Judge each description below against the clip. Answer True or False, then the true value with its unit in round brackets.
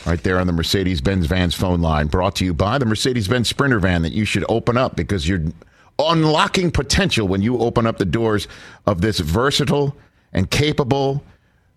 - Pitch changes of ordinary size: False (6.0 semitones)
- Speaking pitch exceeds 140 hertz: False (105 Hz)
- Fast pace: False (195 wpm)